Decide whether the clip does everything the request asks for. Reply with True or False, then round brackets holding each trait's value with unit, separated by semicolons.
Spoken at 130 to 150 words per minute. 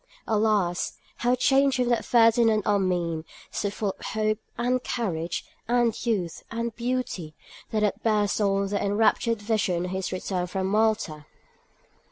True (145 wpm)